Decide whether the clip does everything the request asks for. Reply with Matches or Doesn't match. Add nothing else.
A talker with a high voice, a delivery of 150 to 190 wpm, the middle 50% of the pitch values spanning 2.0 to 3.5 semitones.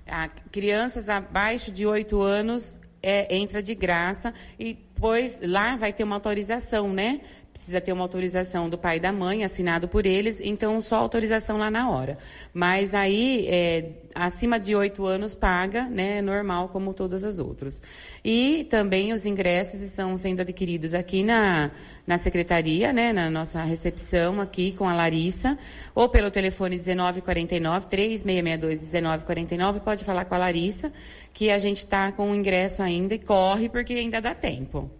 Matches